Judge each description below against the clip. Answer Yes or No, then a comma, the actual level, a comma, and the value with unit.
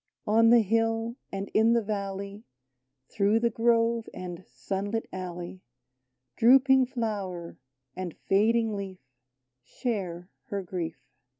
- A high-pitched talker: Yes, high, 210 Hz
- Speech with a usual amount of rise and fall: Yes, average, 3.4 semitones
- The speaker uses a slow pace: Yes, slow, 115 wpm